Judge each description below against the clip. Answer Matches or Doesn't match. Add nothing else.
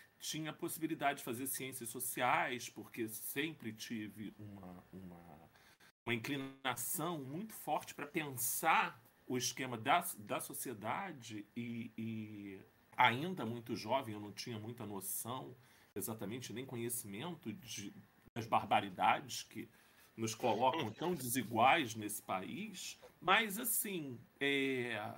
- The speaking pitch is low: Matches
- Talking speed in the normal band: Doesn't match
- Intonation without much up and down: Doesn't match